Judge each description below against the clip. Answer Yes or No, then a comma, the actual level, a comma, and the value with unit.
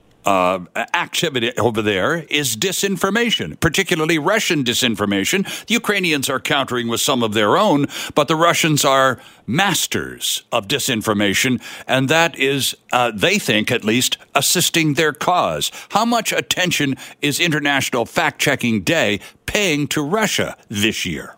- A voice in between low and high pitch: Yes, medium, 145 Hz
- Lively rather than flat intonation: Yes, wide, 5.8 semitones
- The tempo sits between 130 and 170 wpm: Yes, average, 140 wpm